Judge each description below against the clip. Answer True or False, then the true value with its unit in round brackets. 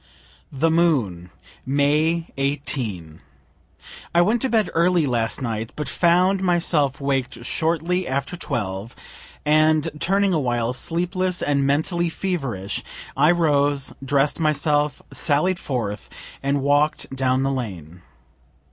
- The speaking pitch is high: False (145 Hz)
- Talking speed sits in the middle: False (115 wpm)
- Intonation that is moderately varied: True (4.6 semitones)